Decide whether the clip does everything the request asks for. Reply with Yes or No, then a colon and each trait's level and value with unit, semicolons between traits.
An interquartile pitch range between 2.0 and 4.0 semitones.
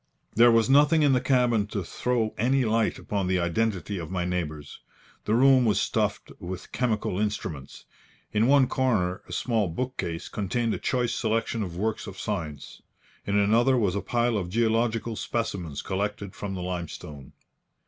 No: average, 4.6 semitones